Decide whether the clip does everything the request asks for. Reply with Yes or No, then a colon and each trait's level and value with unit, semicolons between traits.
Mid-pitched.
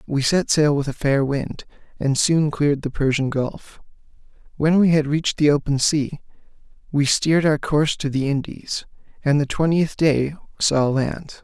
Yes: medium, 145 Hz